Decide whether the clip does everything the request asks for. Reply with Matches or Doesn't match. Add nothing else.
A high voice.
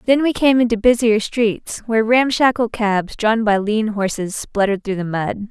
Matches